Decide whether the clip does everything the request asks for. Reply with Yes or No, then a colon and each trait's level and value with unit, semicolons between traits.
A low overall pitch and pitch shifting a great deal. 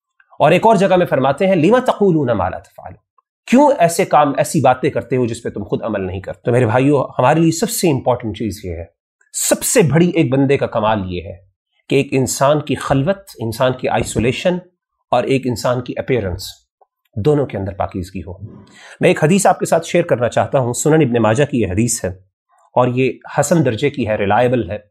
Yes: low, 130 Hz; wide, 6.4 semitones